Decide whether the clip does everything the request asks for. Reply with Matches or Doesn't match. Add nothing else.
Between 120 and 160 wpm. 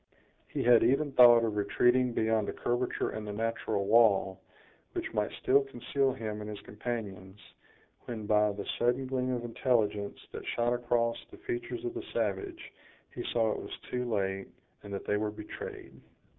Doesn't match